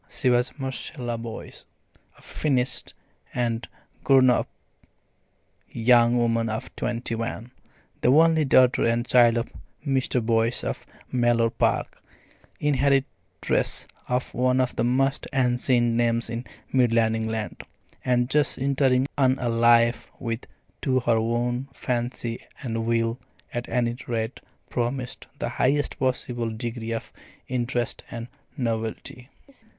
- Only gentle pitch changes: Yes, narrow, 1.8 semitones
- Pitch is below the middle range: Yes, low, 120 Hz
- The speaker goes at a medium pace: No, slow, 125 wpm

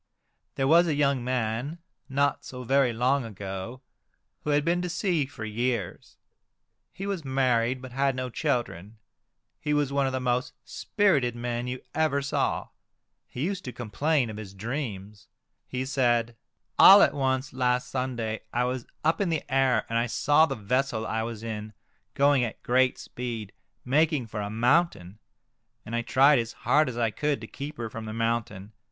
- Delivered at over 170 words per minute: Yes, average, 180 wpm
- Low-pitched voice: Yes, low, 125 Hz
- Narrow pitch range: No, average, 3.6 semitones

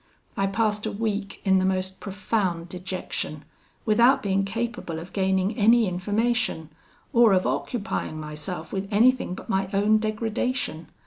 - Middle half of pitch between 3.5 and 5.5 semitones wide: No, average, 3.1 semitones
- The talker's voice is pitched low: No, high, 195 Hz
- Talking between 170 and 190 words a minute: No, average, 140 wpm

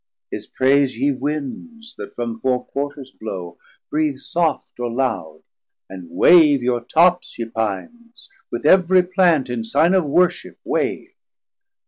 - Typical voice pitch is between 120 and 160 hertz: Yes, medium, 140 Hz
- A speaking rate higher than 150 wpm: No, slow, 135 wpm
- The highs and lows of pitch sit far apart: Yes, wide, 6.4 semitones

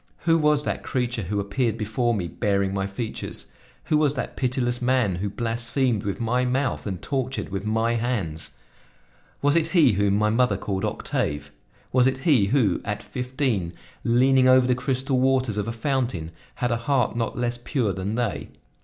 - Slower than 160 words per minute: No, average, 180 wpm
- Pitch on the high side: No, low, 120 Hz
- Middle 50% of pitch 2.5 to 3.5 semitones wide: No, average, 4.2 semitones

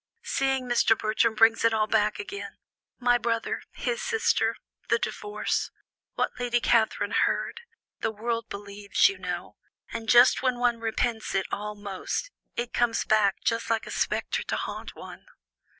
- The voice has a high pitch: Yes, high, 230 Hz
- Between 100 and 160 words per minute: Yes, average, 155 wpm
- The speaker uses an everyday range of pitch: No, narrow, 2.1 semitones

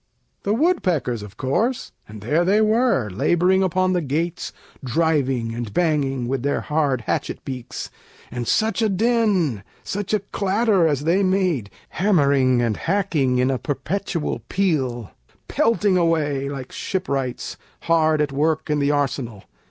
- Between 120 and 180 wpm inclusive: Yes, average, 145 wpm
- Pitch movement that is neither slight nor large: No, wide, 6.4 semitones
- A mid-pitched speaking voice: Yes, medium, 155 Hz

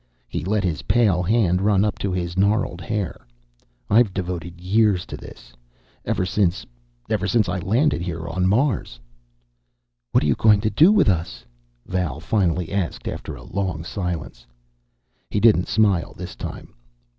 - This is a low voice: Yes, very low, 95 Hz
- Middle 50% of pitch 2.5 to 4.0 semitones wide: Yes, average, 3.3 semitones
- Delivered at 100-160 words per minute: Yes, average, 155 wpm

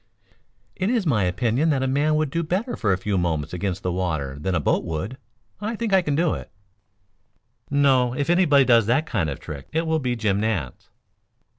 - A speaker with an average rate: No, fast, 210 wpm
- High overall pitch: No, low, 125 Hz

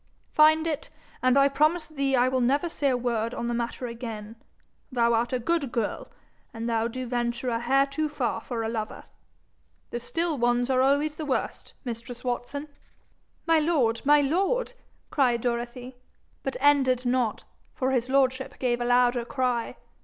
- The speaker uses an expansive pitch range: No, average, 2.8 semitones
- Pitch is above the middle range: Yes, very high, 255 Hz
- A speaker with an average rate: Yes, average, 170 wpm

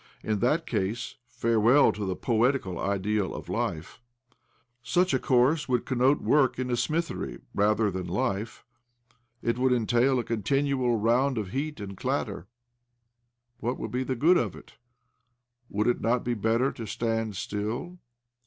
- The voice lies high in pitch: No, low, 120 Hz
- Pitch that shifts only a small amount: No, average, 3.7 semitones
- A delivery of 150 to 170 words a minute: Yes, average, 160 wpm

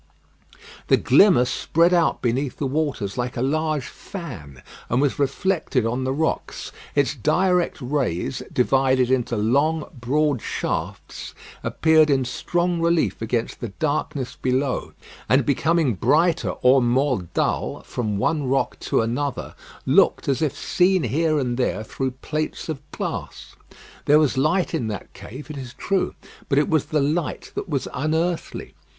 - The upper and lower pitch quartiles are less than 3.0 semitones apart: No, average, 4.1 semitones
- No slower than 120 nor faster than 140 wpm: No, average, 150 wpm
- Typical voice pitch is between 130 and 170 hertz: Yes, medium, 140 Hz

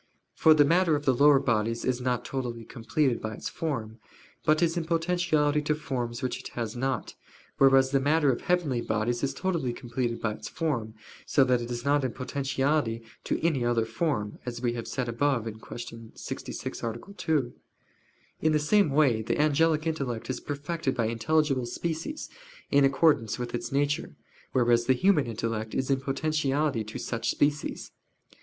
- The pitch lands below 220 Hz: Yes, low, 135 Hz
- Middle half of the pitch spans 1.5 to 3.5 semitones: No, average, 4.3 semitones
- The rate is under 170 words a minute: No, average, 175 wpm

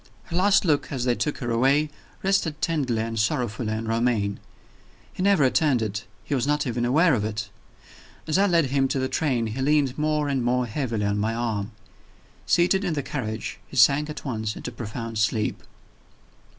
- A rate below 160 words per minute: No, average, 190 wpm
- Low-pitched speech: Yes, low, 125 Hz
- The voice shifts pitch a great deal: No, average, 4.9 semitones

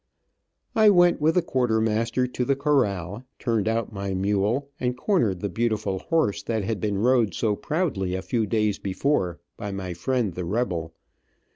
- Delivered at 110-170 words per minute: Yes, average, 165 wpm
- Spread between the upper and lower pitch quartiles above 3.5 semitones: Yes, average, 4.6 semitones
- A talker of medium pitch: No, low, 110 Hz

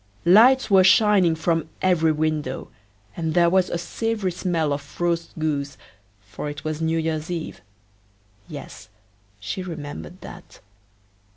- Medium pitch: Yes, medium, 165 Hz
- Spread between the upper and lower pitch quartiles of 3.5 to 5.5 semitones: No, average, 3.0 semitones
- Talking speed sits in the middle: No, slow, 130 wpm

